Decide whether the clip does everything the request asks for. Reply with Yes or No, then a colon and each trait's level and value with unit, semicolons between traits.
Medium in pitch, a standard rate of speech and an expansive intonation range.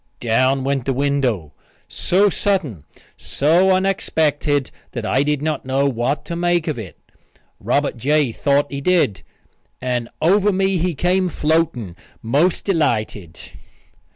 No: medium, 145 Hz; slow, 130 wpm; wide, 5.7 semitones